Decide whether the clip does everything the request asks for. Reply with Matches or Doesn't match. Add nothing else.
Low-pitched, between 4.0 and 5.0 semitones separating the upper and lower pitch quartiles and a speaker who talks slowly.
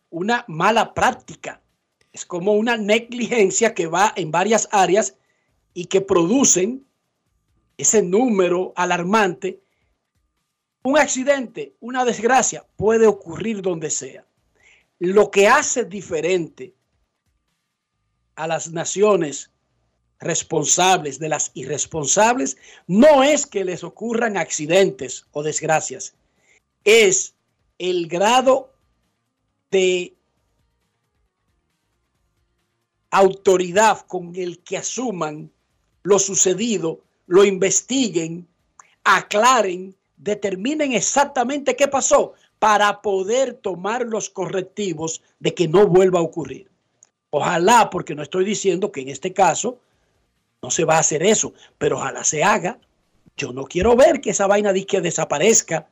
Doesn't match